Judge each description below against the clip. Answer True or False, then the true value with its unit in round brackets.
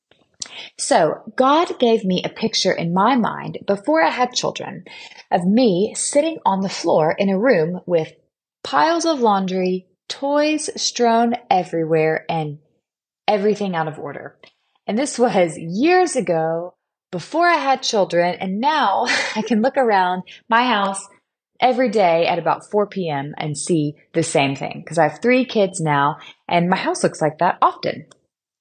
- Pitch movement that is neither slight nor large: False (6.5 semitones)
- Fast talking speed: False (155 wpm)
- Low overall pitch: False (195 Hz)